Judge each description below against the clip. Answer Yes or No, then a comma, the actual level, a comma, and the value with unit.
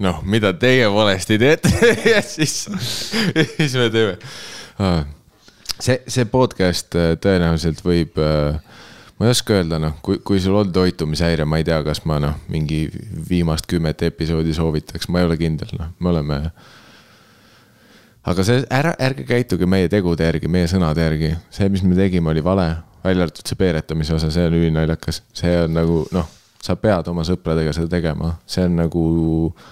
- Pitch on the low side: Yes, very low, 85 Hz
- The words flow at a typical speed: Yes, average, 165 wpm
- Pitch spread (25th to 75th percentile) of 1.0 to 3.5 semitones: No, average, 3.9 semitones